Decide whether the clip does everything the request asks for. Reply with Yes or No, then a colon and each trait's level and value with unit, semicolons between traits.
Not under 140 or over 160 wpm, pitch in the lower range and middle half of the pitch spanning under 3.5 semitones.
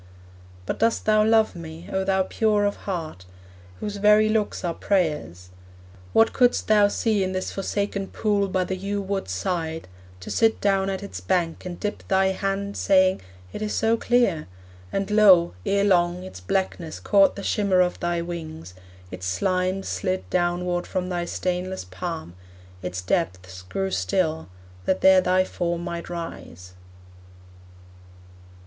No: average, 155 wpm; medium, 185 Hz; average, 2.9 semitones